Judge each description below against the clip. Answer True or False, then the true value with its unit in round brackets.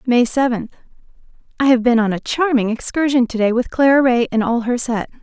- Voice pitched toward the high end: True (245 Hz)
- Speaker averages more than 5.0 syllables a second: True (5.6 syllables/s)